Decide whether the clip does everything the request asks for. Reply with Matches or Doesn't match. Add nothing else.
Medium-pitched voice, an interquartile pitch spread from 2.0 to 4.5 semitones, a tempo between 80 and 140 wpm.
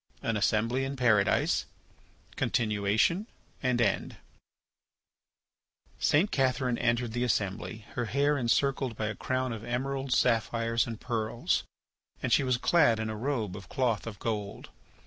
Doesn't match